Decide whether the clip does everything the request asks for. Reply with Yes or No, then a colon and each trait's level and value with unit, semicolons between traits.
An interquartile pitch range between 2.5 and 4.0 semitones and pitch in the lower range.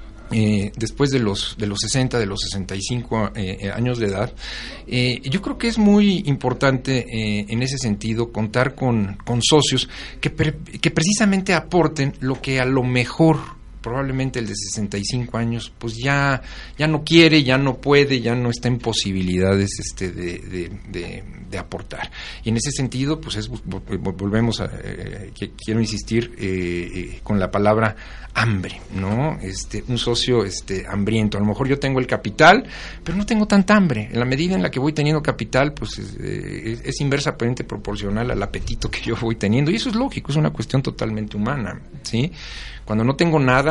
No: average, 4.8 semitones; low, 120 Hz